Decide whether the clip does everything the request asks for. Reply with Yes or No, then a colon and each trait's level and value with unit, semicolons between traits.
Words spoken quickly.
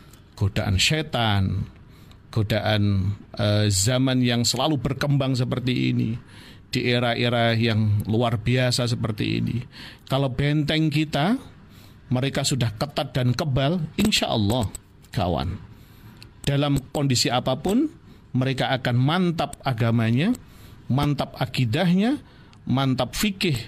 No: average, 100 wpm